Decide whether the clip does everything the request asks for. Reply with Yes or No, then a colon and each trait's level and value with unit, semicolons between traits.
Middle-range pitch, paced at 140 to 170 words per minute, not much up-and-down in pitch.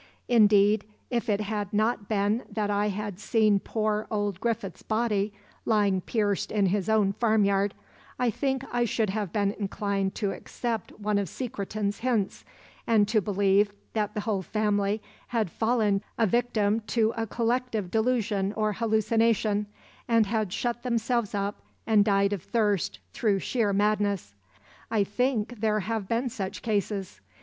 No: high, 210 Hz; average, 150 wpm; narrow, 1.9 semitones